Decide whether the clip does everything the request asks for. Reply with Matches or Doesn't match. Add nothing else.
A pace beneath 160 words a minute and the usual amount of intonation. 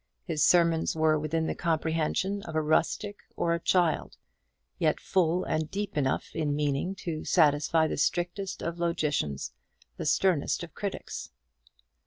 Doesn't match